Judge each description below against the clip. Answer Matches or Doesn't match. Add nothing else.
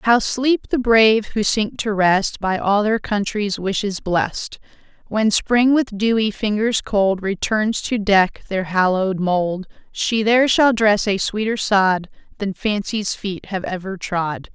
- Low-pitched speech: Doesn't match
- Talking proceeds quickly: Doesn't match